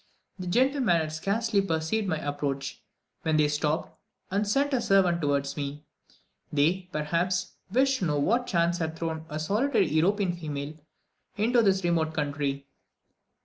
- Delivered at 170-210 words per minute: No, average, 145 wpm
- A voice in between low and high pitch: Yes, medium, 170 Hz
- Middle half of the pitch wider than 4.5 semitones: Yes, average, 4.9 semitones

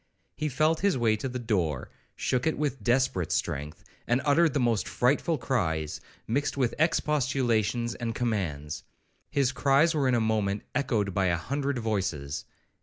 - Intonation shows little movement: No, wide, 5.5 semitones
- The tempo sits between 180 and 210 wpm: No, average, 160 wpm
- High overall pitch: No, low, 120 Hz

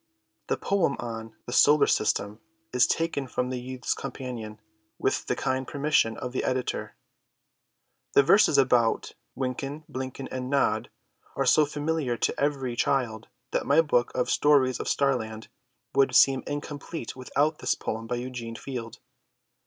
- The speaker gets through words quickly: No, average, 145 wpm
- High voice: No, low, 130 Hz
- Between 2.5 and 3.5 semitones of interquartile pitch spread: Yes, average, 3.0 semitones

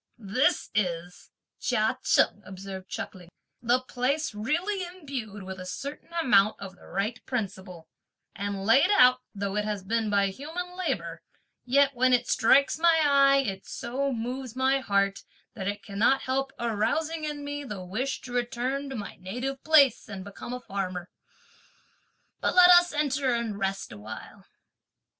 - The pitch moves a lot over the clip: Yes, wide, 5.8 semitones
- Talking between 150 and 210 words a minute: Yes, average, 155 wpm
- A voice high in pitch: Yes, high, 240 Hz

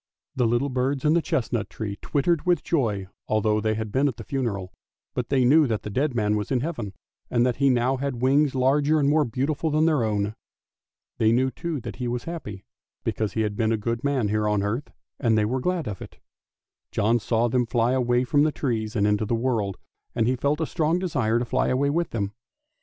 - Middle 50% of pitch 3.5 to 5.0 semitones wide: Yes, average, 4.5 semitones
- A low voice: Yes, low, 125 Hz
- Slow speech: No, fast, 225 wpm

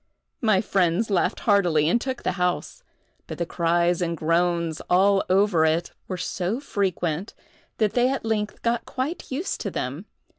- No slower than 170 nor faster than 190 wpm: No, average, 160 wpm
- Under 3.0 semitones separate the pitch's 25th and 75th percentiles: No, average, 4.2 semitones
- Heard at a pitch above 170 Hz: Yes, medium, 185 Hz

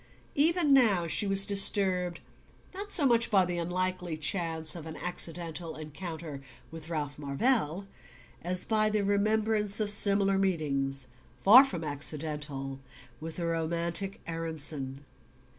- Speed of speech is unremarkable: No, slow, 125 wpm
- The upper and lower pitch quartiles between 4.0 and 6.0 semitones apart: Yes, average, 4.4 semitones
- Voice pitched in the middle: Yes, medium, 175 Hz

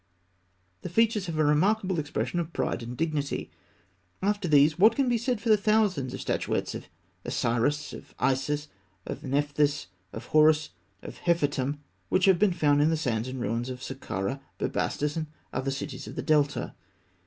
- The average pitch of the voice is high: No, medium, 150 Hz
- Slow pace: No, average, 170 wpm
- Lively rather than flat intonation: No, average, 4.9 semitones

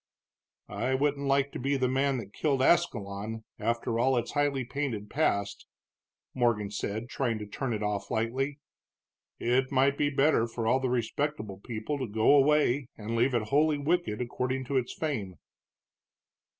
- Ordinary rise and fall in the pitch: Yes, average, 4.0 semitones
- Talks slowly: No, average, 165 wpm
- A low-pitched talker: Yes, low, 130 Hz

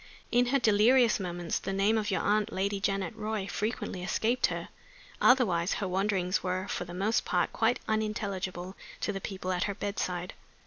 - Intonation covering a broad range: No, average, 2.8 semitones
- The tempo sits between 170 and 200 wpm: Yes, average, 175 wpm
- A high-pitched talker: Yes, high, 200 Hz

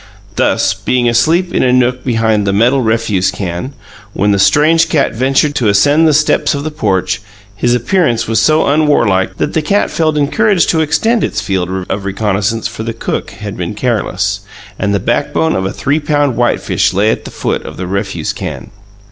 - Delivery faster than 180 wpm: Yes, average, 190 wpm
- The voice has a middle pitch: No, low, 115 Hz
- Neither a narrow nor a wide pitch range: No, wide, 6.7 semitones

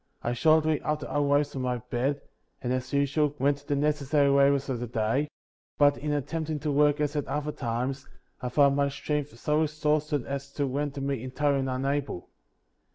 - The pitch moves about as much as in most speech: No, narrow, 1.8 semitones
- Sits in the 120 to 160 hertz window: Yes, medium, 140 Hz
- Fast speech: No, average, 185 wpm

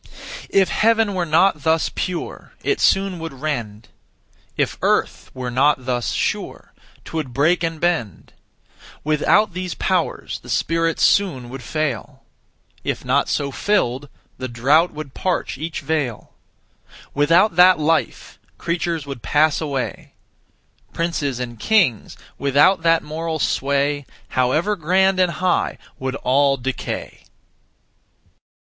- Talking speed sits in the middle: No, slow, 125 wpm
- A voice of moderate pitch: Yes, medium, 155 Hz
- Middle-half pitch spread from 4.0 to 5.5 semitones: Yes, average, 4.5 semitones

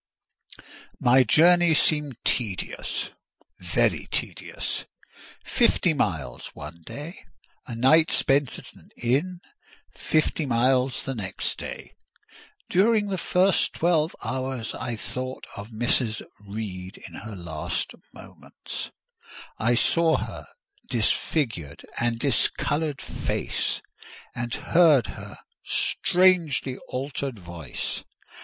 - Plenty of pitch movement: Yes, wide, 5.9 semitones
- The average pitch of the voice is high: No, low, 130 Hz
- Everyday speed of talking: No, slow, 100 wpm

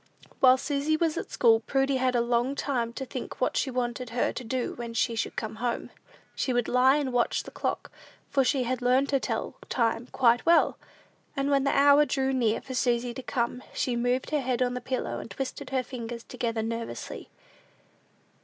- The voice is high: Yes, very high, 250 Hz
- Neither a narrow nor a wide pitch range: No, narrow, 2.1 semitones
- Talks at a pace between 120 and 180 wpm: No, fast, 205 wpm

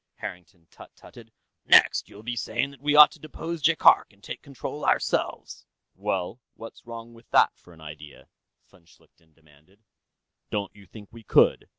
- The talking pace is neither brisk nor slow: Yes, average, 170 wpm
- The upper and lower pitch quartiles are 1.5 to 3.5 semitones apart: No, wide, 5.6 semitones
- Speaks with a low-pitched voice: Yes, low, 105 Hz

